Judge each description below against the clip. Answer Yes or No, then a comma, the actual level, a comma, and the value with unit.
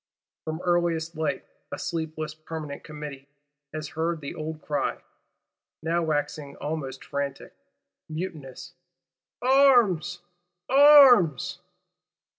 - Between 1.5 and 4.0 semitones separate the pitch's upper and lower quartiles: Yes, narrow, 2.6 semitones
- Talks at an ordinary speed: No, slow, 90 wpm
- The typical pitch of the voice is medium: Yes, medium, 160 Hz